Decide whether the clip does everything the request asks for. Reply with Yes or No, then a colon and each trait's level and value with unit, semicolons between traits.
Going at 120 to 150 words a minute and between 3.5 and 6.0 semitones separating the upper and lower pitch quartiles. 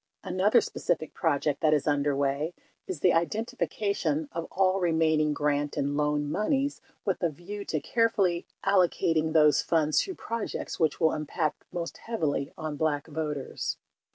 Yes: average, 145 wpm; average, 3.9 semitones